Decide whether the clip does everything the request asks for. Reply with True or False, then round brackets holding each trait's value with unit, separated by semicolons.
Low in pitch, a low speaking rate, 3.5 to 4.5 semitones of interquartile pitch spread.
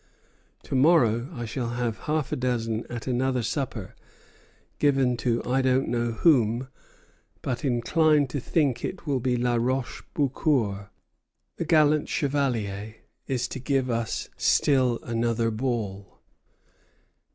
False (125 Hz; 130 wpm; 2.8 semitones)